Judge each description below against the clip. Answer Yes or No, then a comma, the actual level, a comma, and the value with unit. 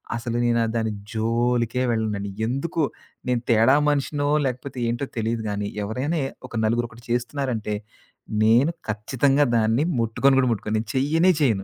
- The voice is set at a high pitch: No, low, 120 Hz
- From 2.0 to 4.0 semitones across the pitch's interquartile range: Yes, average, 3.3 semitones